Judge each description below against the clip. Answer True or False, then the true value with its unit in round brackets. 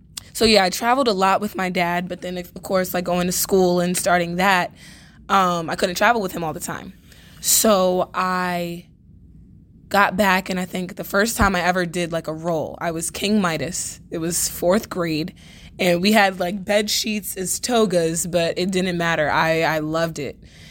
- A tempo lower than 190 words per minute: False (200 wpm)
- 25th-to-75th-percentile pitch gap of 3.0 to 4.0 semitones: False (2.5 semitones)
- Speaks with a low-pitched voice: False (180 Hz)